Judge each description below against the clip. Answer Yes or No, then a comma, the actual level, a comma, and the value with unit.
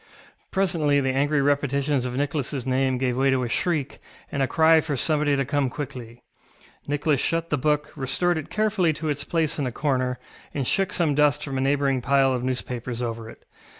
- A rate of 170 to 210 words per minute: Yes, average, 195 wpm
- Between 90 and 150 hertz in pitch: Yes, medium, 140 Hz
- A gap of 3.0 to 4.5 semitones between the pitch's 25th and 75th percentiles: No, narrow, 2.6 semitones